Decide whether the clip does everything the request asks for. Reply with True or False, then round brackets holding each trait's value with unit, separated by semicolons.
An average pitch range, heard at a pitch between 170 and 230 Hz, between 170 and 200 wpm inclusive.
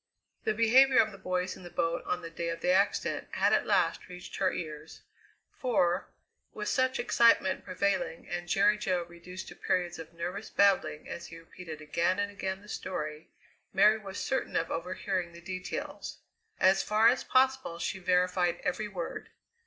True (3.0 semitones; 185 Hz; 175 wpm)